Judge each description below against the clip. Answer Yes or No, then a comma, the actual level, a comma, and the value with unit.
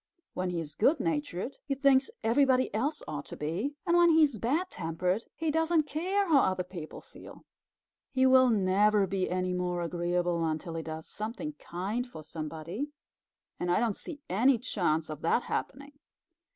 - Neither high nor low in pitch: No, high, 210 Hz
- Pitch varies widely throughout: Yes, wide, 8.0 semitones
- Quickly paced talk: No, average, 175 wpm